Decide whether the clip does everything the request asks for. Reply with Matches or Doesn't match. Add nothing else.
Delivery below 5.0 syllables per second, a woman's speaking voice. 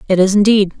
Doesn't match